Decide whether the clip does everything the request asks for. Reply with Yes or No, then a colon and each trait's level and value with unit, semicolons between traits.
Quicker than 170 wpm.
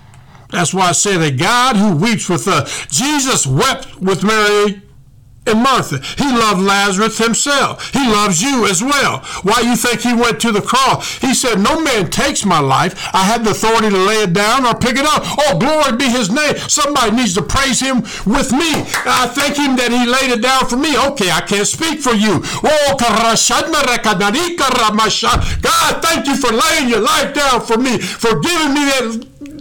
Yes: average, 195 wpm